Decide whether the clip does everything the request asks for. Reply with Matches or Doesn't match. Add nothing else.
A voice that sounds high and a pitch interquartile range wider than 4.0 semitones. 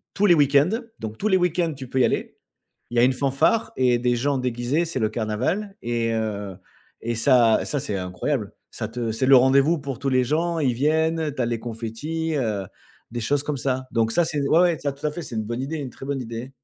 Doesn't match